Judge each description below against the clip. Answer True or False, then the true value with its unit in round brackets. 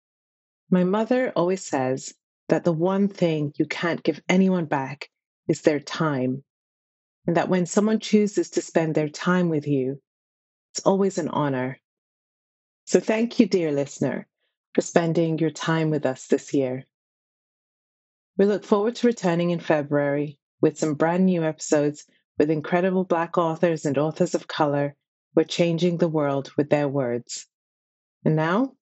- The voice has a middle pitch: True (160 Hz)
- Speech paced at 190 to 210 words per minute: False (155 wpm)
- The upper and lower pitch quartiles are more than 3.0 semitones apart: True (4.2 semitones)